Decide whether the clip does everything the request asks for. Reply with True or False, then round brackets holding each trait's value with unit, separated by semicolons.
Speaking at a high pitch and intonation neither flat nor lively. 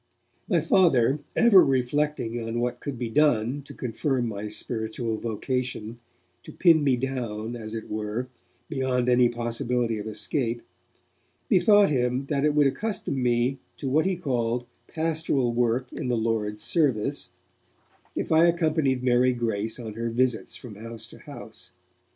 False (125 Hz; 3.8 semitones)